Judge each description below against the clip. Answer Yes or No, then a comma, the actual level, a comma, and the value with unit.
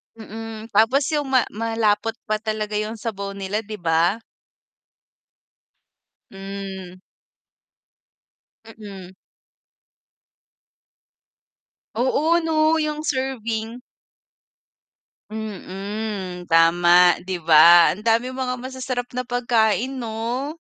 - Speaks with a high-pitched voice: Yes, high, 220 Hz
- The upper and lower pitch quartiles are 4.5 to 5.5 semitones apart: No, average, 4.1 semitones